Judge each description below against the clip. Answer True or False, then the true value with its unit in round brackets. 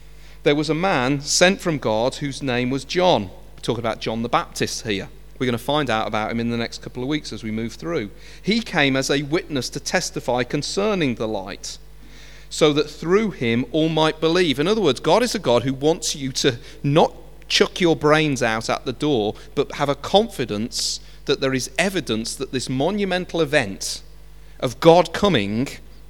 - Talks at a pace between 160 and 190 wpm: False (200 wpm)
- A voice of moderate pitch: True (145 Hz)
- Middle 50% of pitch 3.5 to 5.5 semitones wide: True (4.2 semitones)